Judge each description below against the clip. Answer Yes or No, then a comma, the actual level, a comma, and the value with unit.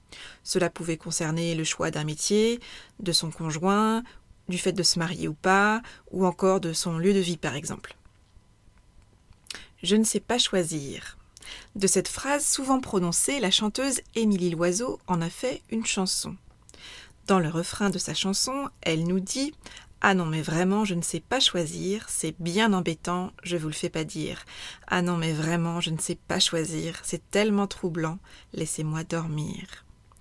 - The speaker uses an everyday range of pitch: Yes, average, 3.6 semitones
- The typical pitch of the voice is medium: Yes, medium, 175 Hz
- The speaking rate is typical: Yes, average, 170 wpm